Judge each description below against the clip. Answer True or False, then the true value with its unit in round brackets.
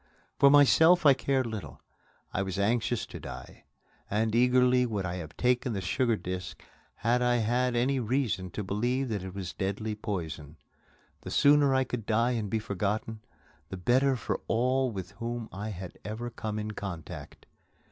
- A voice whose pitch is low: True (115 Hz)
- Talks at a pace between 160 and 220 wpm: True (170 wpm)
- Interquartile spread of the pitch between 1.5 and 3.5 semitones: False (4.1 semitones)